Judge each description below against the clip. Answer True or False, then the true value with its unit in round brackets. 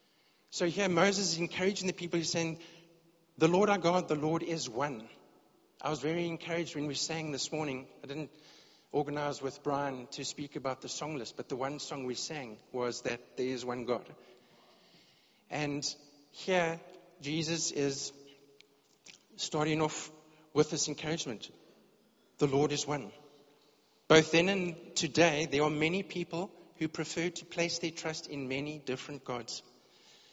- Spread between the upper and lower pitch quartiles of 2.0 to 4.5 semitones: True (2.9 semitones)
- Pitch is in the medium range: True (155 Hz)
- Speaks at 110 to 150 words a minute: False (160 wpm)